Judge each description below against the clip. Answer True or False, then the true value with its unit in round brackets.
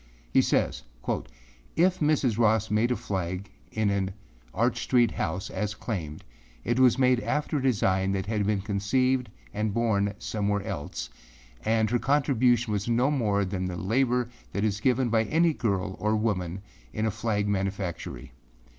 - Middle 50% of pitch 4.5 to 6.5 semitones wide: False (3.7 semitones)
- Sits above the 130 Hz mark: False (110 Hz)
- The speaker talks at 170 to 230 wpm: False (160 wpm)